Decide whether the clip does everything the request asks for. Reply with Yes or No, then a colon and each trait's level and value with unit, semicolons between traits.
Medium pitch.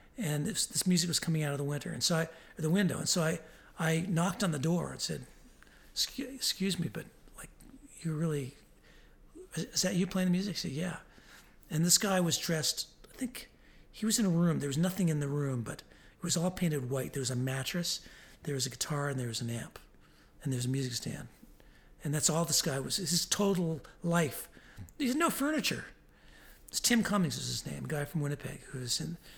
Yes: medium, 165 Hz